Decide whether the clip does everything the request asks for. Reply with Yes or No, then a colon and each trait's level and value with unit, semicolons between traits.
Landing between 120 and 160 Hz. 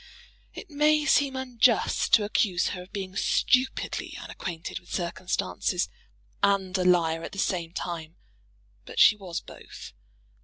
No: high, 190 Hz